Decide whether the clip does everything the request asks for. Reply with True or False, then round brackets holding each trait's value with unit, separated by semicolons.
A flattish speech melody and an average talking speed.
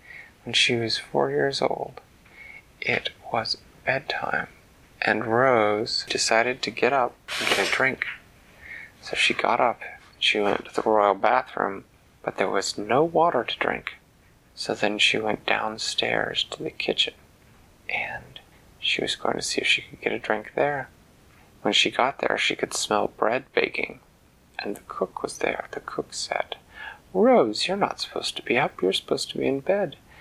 False (3.5 semitones; 175 wpm)